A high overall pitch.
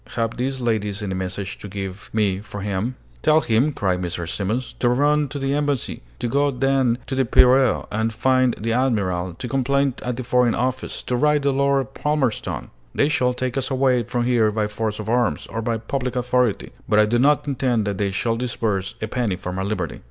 No: low, 120 Hz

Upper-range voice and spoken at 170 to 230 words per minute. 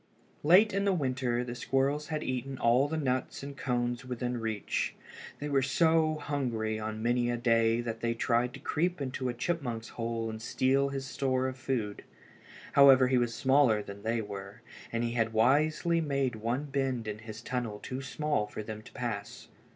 No: low, 125 Hz; average, 185 wpm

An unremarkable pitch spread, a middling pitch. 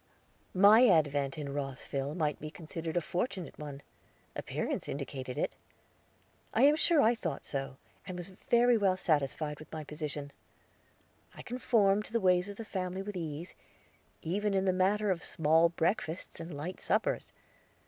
Yes: average, 5.0 semitones; medium, 170 Hz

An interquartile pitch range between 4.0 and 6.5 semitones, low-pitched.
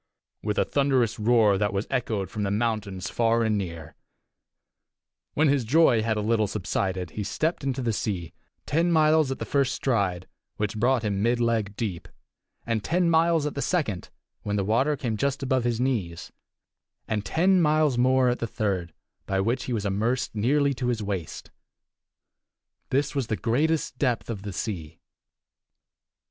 Yes: average, 4.8 semitones; low, 115 Hz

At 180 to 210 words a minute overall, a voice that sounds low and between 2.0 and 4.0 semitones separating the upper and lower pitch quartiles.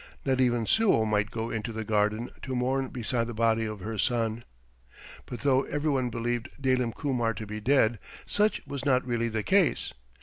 Yes: average, 190 wpm; low, 120 Hz; average, 2.8 semitones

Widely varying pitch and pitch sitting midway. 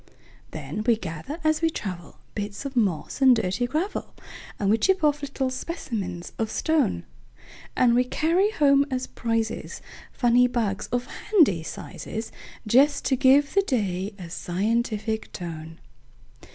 No: wide, 5.8 semitones; high, 240 Hz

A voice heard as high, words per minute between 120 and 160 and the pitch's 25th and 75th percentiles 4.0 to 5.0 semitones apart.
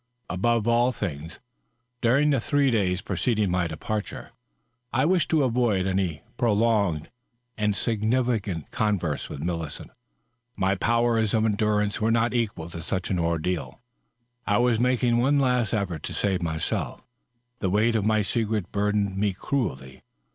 No: low, 105 Hz; average, 145 wpm; average, 4.3 semitones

